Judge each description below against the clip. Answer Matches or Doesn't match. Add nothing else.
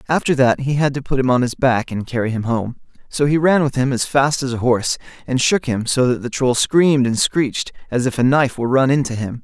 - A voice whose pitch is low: Matches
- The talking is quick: Matches